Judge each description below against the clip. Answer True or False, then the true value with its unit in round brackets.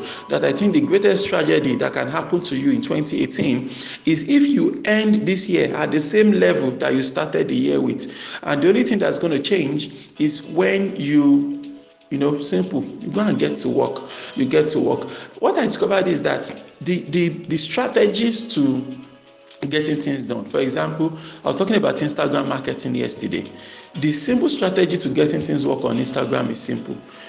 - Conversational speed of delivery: True (185 wpm)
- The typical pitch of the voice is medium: True (175 Hz)